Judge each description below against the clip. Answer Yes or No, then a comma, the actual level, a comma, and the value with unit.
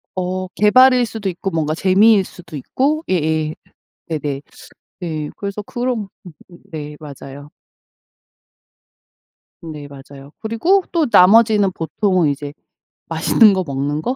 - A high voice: No, medium, 180 Hz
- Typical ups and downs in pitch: No, wide, 6.2 semitones